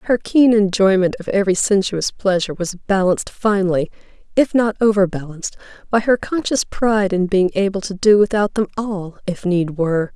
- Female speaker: Yes, female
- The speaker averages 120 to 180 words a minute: Yes, average, 165 wpm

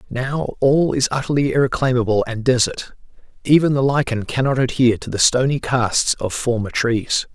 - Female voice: No, male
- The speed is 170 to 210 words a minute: No, average, 155 wpm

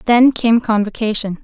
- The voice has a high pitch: Yes, high, 225 Hz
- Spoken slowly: Yes, slow, 125 wpm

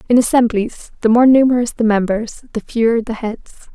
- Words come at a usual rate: Yes, average, 175 wpm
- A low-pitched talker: No, high, 230 Hz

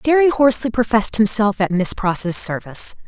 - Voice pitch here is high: Yes, high, 220 Hz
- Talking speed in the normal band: Yes, average, 155 wpm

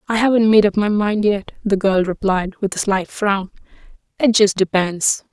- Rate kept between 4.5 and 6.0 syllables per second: Yes, 4.8 syllables/s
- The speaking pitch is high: Yes, high, 200 Hz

